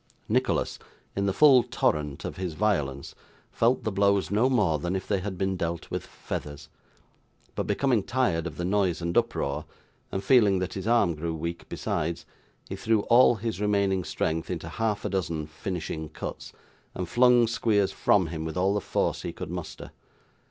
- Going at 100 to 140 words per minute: No, average, 180 wpm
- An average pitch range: Yes, average, 4.4 semitones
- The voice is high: No, very low, 95 Hz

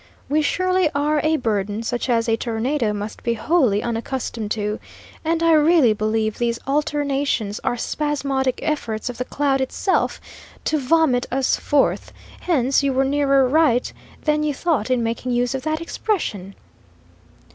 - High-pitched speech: Yes, very high, 265 Hz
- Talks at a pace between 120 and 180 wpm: Yes, average, 155 wpm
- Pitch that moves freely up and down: No, average, 4.7 semitones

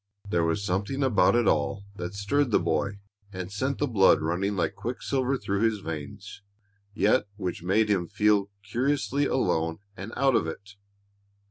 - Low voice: Yes, low, 100 Hz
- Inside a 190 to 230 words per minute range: No, average, 165 wpm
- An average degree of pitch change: Yes, average, 4.4 semitones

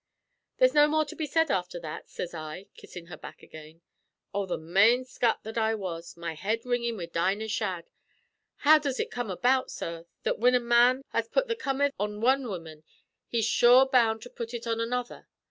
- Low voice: No, high, 230 Hz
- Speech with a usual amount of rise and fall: No, wide, 5.8 semitones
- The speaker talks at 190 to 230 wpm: Yes, average, 200 wpm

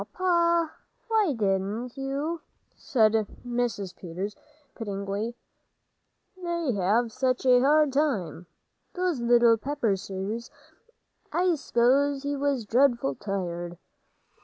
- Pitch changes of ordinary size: No, wide, 6.0 semitones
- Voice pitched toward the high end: Yes, high, 240 Hz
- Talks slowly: Yes, slow, 100 wpm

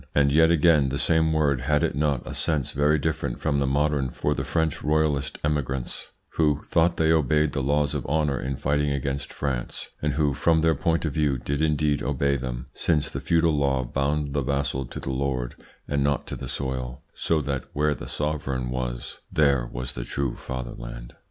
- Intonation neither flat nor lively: No, narrow, 2.3 semitones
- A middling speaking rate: Yes, average, 195 wpm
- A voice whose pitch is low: Yes, very low, 70 Hz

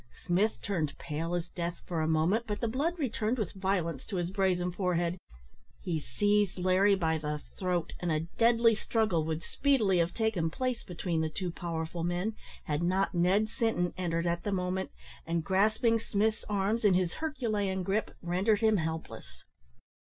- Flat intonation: No, average, 4.0 semitones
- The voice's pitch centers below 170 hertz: No, medium, 185 Hz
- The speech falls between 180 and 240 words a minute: No, average, 170 wpm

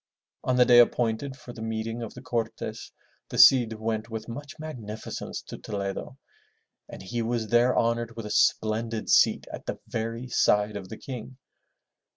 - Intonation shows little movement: Yes, narrow, 1.7 semitones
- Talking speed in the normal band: Yes, average, 170 wpm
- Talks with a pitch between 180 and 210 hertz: No, low, 115 Hz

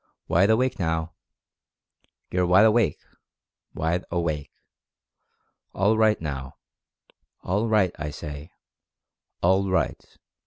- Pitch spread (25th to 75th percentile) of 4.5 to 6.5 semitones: Yes, average, 4.8 semitones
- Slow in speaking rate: Yes, slow, 110 wpm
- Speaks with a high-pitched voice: No, very low, 90 Hz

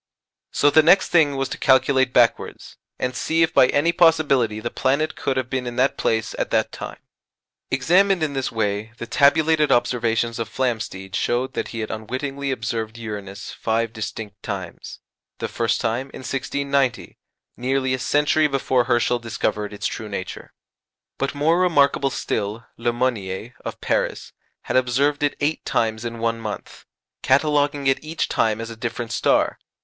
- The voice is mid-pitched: No, low, 125 Hz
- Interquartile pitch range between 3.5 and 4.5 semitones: Yes, average, 3.9 semitones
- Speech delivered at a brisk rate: No, average, 165 wpm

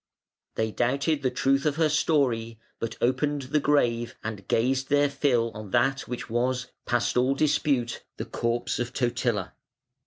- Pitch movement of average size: Yes, average, 3.0 semitones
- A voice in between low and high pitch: No, low, 130 Hz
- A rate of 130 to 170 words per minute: Yes, average, 155 wpm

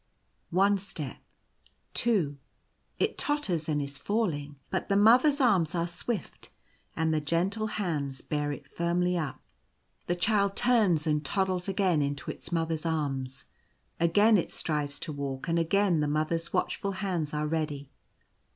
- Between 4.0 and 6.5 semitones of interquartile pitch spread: Yes, average, 4.9 semitones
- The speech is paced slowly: No, average, 155 wpm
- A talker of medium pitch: Yes, medium, 165 Hz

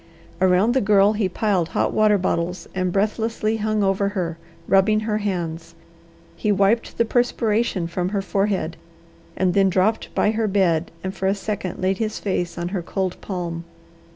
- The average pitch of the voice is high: Yes, high, 195 Hz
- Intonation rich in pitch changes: No, average, 2.8 semitones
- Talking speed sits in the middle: Yes, average, 170 wpm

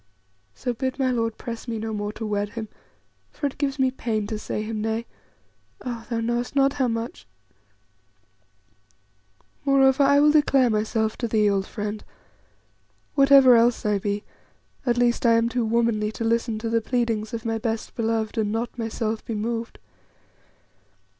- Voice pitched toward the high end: Yes, high, 230 Hz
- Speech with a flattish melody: Yes, narrow, 2.2 semitones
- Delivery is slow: No, average, 165 wpm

